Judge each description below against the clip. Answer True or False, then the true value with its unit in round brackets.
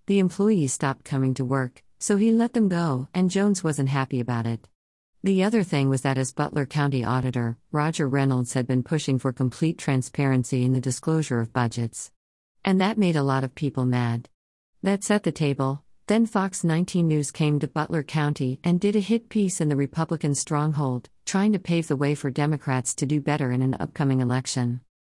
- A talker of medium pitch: True (145 Hz)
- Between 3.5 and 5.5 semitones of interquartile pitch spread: True (4.7 semitones)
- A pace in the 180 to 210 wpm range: True (195 wpm)